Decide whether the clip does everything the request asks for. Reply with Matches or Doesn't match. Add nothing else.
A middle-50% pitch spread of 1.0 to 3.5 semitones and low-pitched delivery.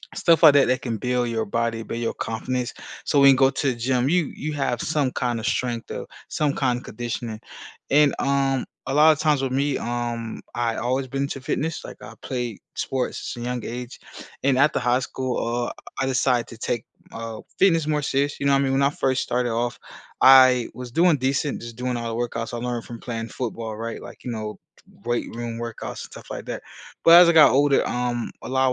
Matches